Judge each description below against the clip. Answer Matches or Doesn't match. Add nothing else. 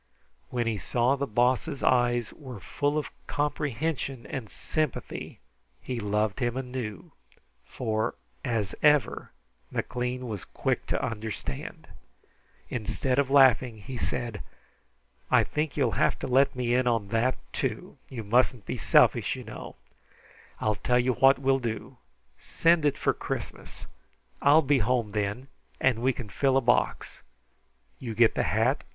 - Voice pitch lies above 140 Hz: Doesn't match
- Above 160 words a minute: Doesn't match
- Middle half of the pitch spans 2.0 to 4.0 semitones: Matches